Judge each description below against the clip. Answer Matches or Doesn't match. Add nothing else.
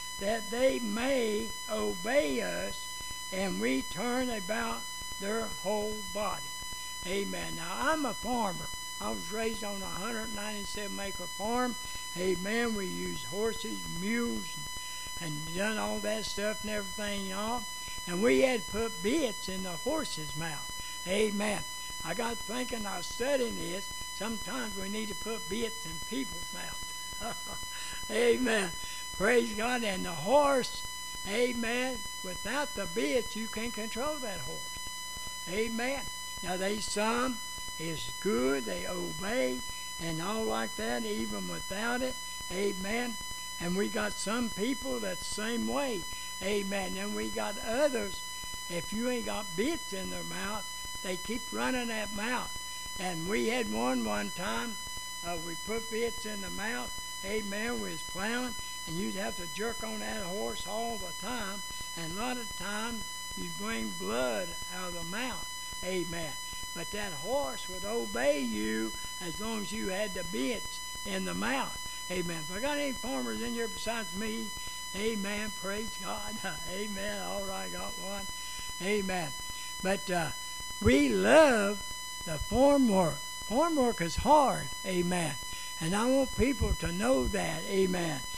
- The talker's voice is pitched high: Matches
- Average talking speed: Matches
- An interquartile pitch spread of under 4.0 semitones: Doesn't match